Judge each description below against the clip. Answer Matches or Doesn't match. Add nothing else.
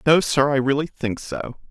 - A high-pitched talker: Doesn't match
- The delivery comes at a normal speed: Doesn't match